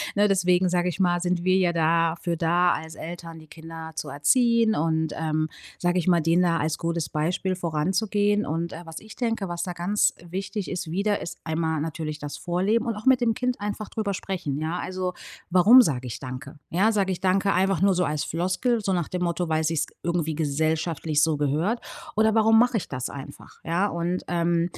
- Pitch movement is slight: No, average, 3.4 semitones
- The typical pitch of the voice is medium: Yes, medium, 175 Hz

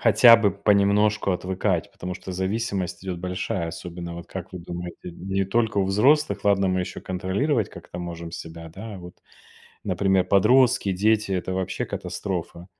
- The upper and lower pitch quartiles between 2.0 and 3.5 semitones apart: Yes, average, 2.7 semitones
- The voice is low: Yes, very low, 95 Hz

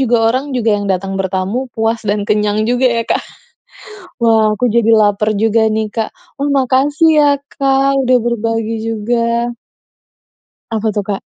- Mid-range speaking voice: No, high, 225 Hz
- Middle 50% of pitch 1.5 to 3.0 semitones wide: Yes, average, 2.7 semitones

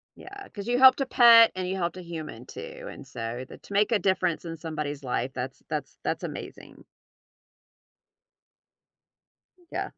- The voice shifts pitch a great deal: Yes, wide, 8.2 semitones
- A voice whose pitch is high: No, medium, 175 Hz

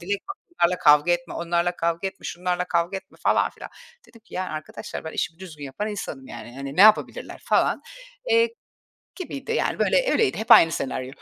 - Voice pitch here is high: No, medium, 175 Hz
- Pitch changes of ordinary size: Yes, average, 4.8 semitones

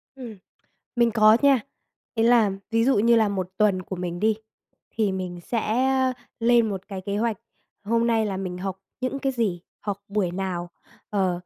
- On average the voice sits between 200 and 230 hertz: Yes, high, 210 Hz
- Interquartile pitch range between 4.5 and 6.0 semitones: No, average, 3.6 semitones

